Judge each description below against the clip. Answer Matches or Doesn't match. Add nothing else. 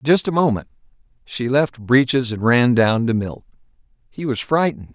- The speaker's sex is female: Doesn't match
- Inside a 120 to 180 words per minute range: Matches